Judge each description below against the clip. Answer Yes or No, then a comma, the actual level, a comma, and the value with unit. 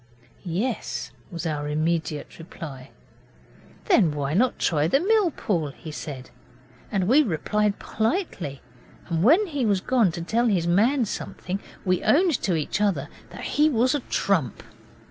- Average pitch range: No, wide, 7.8 semitones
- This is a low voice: No, high, 190 Hz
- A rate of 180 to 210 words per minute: No, average, 150 wpm